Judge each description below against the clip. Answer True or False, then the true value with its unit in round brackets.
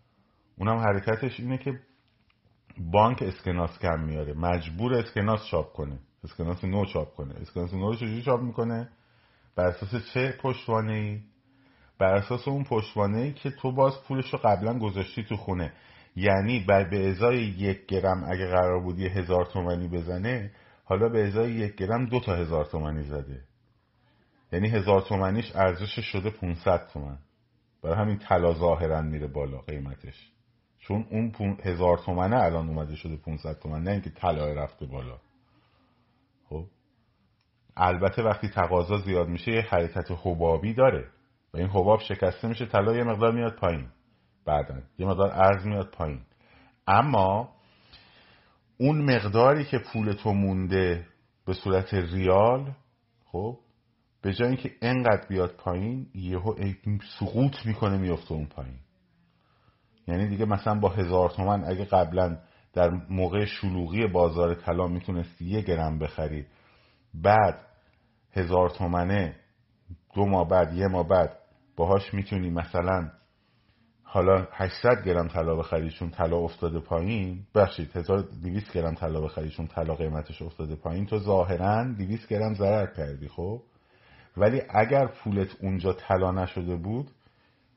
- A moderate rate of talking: True (135 wpm)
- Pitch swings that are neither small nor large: True (4.3 semitones)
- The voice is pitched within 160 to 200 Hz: False (100 Hz)